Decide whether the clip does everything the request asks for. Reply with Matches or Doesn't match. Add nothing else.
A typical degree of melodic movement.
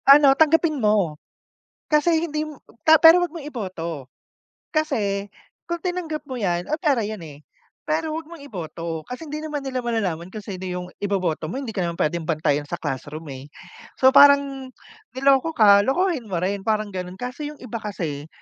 Doesn't match